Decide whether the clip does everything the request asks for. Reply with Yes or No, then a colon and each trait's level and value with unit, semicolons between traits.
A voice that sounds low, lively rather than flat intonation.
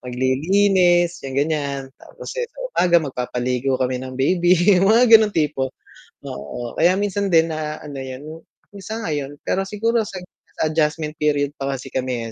No: medium, 150 Hz; wide, 5.9 semitones